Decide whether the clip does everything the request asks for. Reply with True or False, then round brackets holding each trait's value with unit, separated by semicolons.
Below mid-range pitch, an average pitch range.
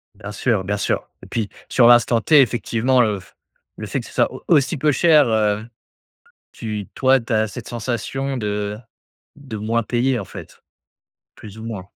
True (115 Hz; 3.6 semitones)